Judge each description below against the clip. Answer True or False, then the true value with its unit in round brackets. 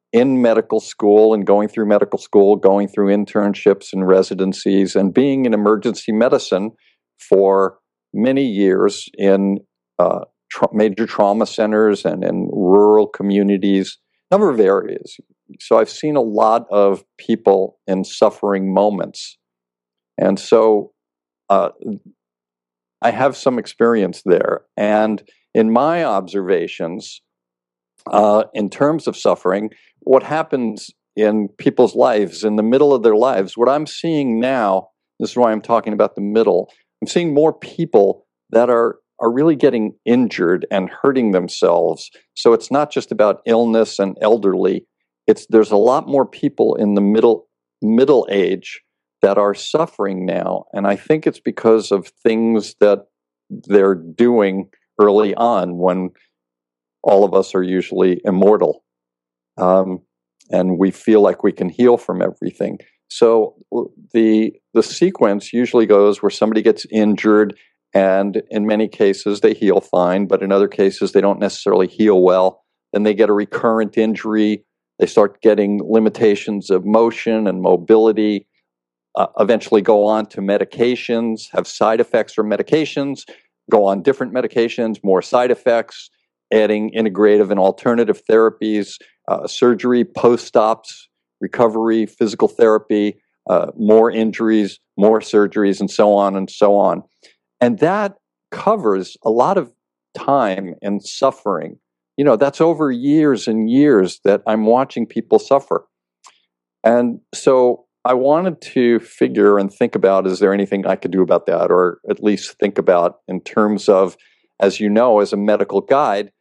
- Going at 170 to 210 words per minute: False (150 wpm)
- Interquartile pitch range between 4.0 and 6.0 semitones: False (3.2 semitones)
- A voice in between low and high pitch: False (105 Hz)